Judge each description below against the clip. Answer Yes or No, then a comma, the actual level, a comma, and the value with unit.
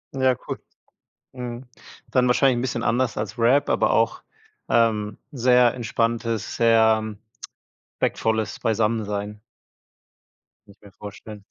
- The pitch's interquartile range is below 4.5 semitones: Yes, narrow, 2.4 semitones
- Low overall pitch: Yes, low, 115 Hz